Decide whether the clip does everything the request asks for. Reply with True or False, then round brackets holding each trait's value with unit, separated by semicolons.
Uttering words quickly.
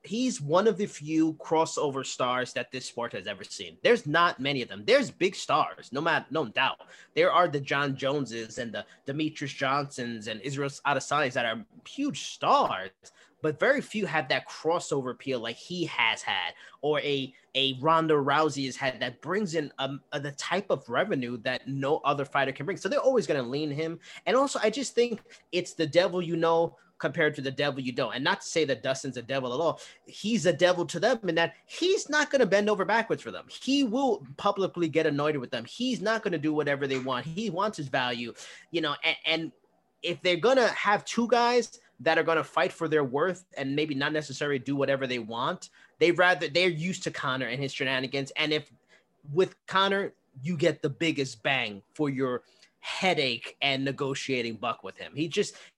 True (210 wpm)